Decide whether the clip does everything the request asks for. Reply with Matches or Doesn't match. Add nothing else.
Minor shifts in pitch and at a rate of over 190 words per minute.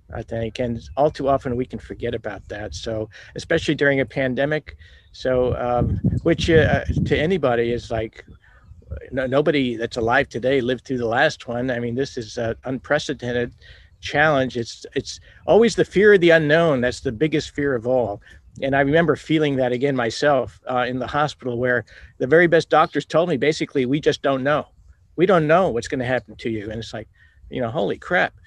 Doesn't match